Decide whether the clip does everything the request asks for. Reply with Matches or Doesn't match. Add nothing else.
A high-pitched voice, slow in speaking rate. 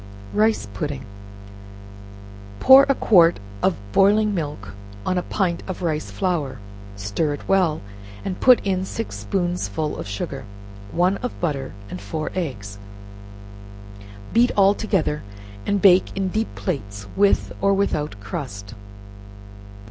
Doesn't match